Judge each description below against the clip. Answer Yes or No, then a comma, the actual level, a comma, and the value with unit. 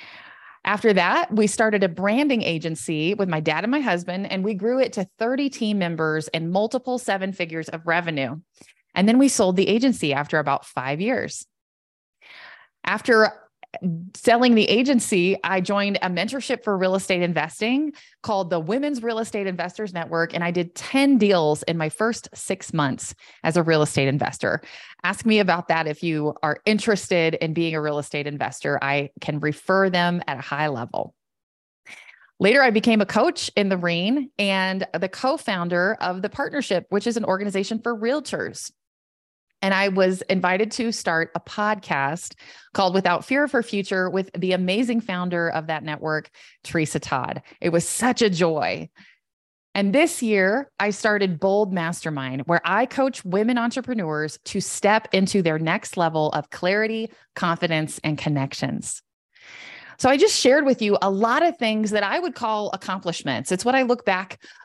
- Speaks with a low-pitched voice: No, high, 190 Hz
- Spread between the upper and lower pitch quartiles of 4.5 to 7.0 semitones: Yes, average, 5.0 semitones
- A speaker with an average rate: Yes, average, 170 wpm